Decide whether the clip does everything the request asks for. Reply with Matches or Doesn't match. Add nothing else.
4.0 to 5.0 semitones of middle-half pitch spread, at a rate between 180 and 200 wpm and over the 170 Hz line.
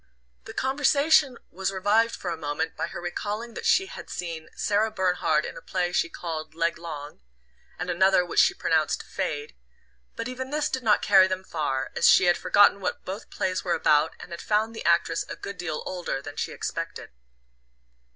Matches